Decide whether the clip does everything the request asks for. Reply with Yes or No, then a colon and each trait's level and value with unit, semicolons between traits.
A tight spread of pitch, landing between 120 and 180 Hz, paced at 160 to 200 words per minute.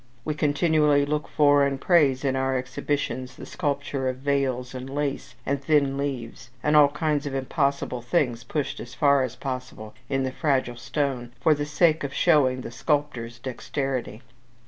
Yes: narrow, 2.2 semitones; medium, 140 Hz; average, 170 wpm